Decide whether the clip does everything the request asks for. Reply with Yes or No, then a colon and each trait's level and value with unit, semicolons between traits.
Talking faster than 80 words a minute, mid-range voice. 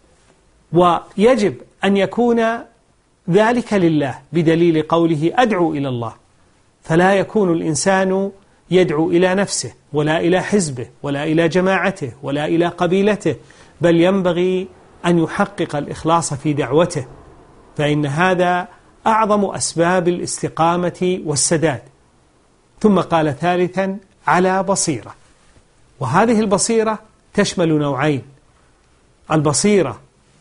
Yes: average, 95 wpm; medium, 170 Hz